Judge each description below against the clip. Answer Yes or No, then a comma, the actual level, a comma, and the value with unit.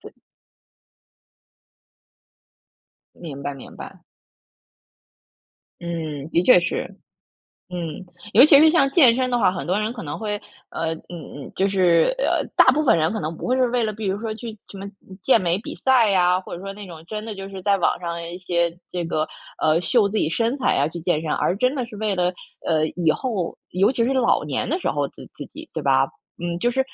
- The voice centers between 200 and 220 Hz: No, high, 190 Hz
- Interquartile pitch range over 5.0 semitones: Yes, wide, 5.5 semitones